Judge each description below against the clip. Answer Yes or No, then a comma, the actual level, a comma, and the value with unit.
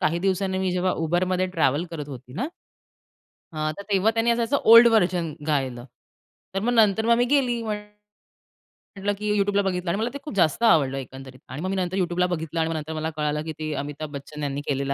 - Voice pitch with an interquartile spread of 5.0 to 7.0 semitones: Yes, wide, 5.5 semitones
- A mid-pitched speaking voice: Yes, medium, 180 Hz